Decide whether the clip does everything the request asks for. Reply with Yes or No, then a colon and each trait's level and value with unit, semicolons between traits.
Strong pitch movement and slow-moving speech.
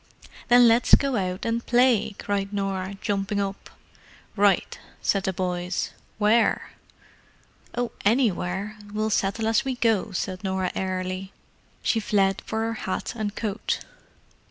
No: average, 2.8 semitones; slow, 130 wpm